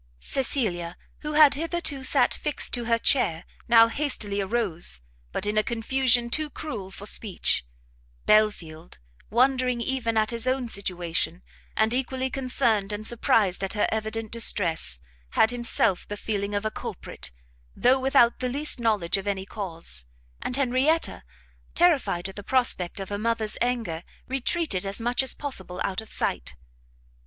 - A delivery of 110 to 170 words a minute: Yes, average, 150 wpm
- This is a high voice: Yes, high, 225 Hz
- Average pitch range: Yes, average, 4.7 semitones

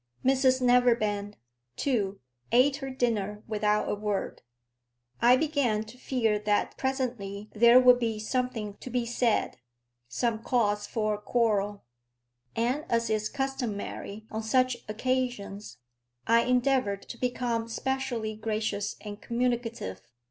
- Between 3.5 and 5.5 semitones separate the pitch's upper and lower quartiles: No, average, 3.1 semitones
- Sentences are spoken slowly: Yes, slow, 125 wpm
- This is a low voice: No, high, 230 Hz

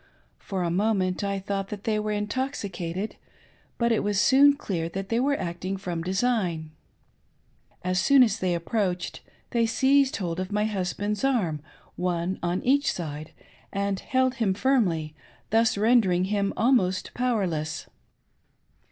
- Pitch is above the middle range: Yes, high, 200 Hz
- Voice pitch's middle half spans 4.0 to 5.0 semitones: Yes, average, 4.3 semitones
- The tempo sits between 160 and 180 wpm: No, average, 145 wpm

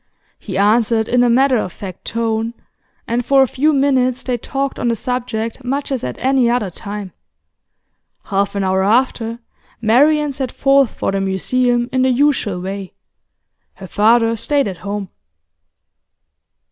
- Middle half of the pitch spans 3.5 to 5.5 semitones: Yes, average, 4.1 semitones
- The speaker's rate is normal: Yes, average, 155 wpm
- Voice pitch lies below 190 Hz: No, high, 235 Hz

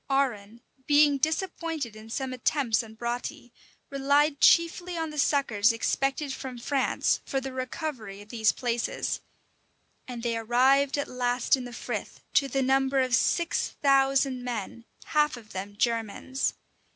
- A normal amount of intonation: Yes, average, 3.1 semitones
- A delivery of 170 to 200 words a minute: No, average, 145 wpm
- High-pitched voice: Yes, very high, 260 Hz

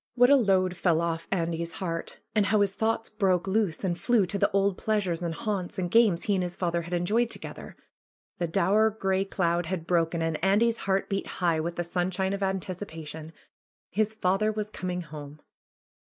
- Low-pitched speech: No, medium, 185 Hz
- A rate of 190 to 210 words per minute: Yes, average, 195 wpm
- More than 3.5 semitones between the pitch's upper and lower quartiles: No, average, 3.2 semitones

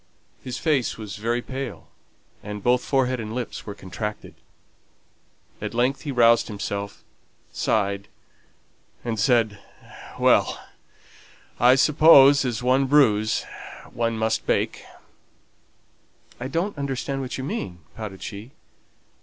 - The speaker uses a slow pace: Yes, slow, 115 wpm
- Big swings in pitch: No, average, 3.9 semitones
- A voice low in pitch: Yes, low, 120 Hz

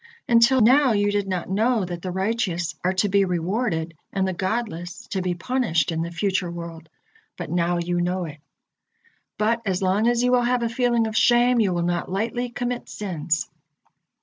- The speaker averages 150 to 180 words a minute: No, average, 190 wpm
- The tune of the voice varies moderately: Yes, average, 5.0 semitones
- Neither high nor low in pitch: No, high, 195 Hz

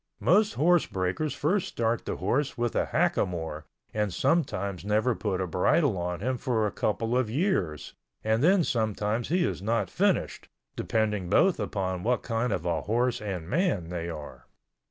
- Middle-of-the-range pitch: No, low, 110 Hz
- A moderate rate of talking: Yes, average, 170 wpm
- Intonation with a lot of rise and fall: Yes, wide, 6.0 semitones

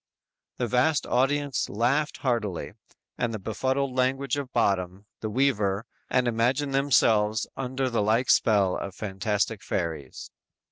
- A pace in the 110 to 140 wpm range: Yes, slow, 135 wpm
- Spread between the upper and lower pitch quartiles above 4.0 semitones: Yes, average, 4.4 semitones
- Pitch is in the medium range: No, low, 120 Hz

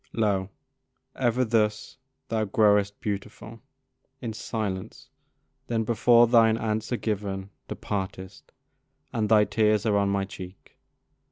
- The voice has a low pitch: Yes, low, 105 Hz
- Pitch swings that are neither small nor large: No, narrow, 2.2 semitones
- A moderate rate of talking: No, slow, 110 wpm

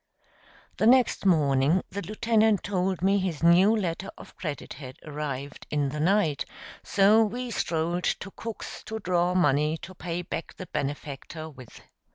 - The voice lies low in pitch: No, medium, 175 Hz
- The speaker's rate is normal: Yes, average, 155 wpm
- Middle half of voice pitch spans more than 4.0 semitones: Yes, average, 4.9 semitones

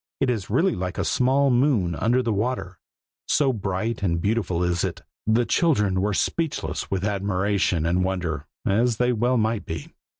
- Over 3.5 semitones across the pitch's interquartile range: Yes, average, 5.1 semitones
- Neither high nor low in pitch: No, low, 105 Hz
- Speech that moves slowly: No, average, 170 wpm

